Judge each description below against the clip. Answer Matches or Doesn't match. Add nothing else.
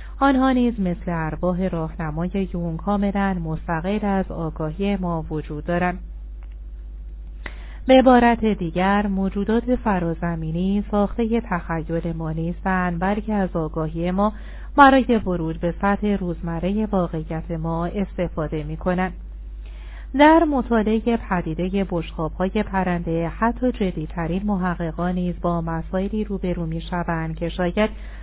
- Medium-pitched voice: Matches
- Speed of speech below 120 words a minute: Matches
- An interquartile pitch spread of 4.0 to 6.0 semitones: Doesn't match